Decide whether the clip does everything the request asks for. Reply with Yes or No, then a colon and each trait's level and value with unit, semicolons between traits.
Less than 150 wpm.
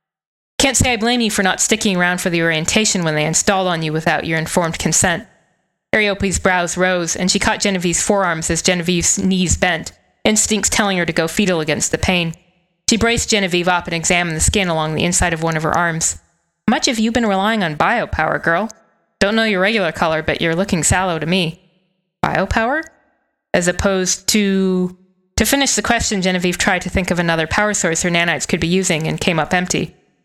No: average, 200 wpm